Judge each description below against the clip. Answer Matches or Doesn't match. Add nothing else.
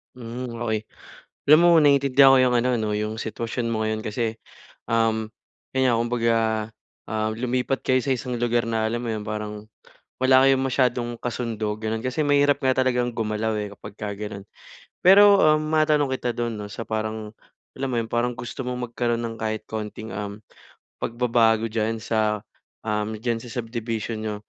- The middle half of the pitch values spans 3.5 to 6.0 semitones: Doesn't match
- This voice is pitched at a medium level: Doesn't match